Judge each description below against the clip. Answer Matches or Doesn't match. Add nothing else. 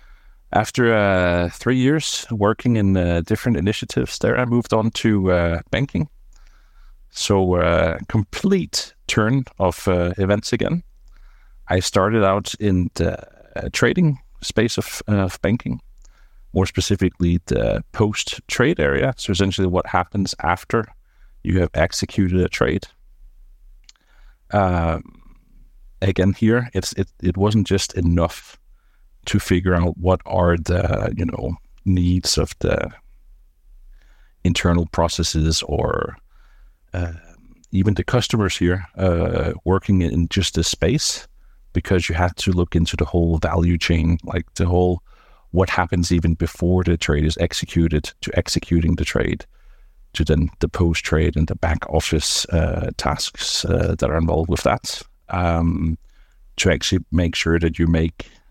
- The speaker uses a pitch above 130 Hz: Doesn't match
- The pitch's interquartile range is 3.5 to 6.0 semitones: Doesn't match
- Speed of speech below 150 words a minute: Matches